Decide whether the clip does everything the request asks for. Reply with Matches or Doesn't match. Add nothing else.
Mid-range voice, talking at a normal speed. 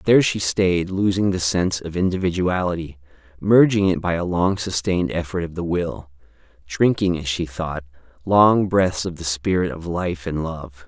Doesn't match